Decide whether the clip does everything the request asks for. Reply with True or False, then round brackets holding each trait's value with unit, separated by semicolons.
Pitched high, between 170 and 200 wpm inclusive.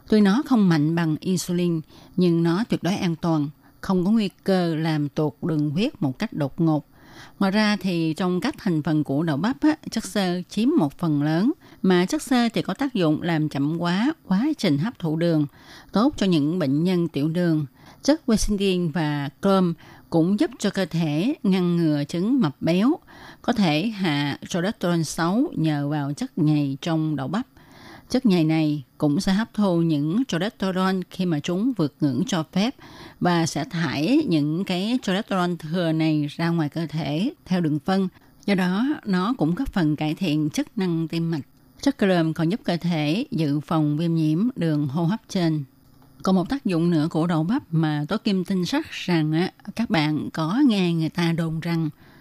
False (170 Hz; 190 wpm)